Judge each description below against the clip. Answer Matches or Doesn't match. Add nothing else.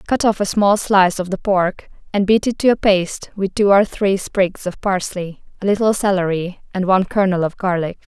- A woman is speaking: Matches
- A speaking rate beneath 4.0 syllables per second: Doesn't match